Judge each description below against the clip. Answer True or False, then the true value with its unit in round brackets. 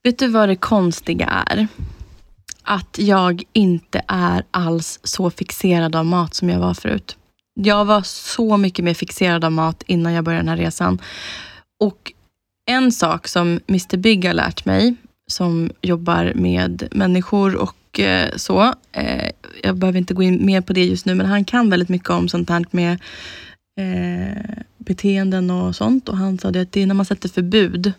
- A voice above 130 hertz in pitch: True (185 Hz)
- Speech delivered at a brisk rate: False (170 wpm)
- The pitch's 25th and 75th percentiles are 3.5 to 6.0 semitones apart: False (2.9 semitones)